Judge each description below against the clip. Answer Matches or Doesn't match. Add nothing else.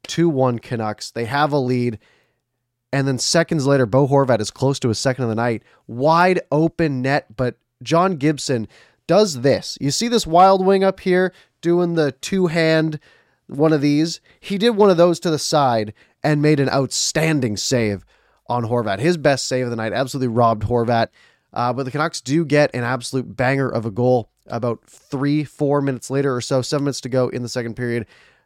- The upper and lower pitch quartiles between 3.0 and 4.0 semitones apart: Doesn't match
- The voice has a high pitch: Doesn't match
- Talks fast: Doesn't match